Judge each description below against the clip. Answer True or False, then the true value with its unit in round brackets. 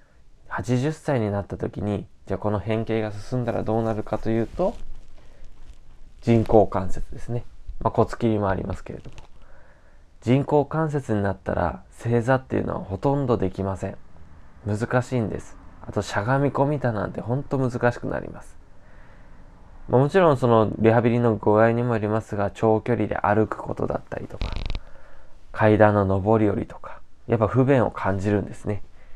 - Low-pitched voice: True (110 Hz)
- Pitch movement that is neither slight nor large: True (3.8 semitones)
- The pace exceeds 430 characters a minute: False (330 characters per minute)